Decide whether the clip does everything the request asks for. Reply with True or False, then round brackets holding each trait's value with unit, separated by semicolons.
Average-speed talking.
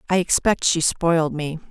True (175 wpm)